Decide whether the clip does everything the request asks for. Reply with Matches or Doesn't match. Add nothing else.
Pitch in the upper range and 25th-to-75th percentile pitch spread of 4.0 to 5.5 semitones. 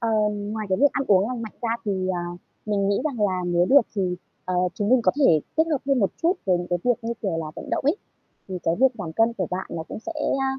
Matches